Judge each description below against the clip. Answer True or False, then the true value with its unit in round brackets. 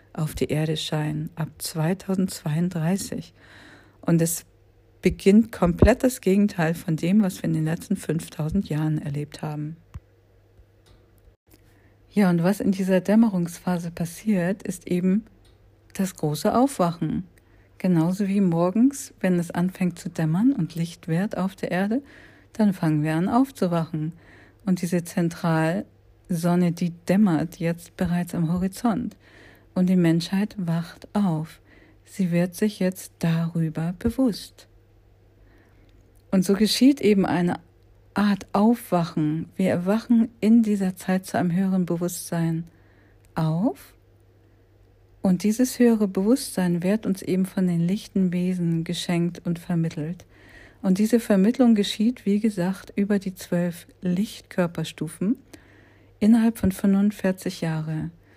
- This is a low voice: False (175 Hz)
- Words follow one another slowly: True (120 wpm)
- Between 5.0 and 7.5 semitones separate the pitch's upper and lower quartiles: False (4.2 semitones)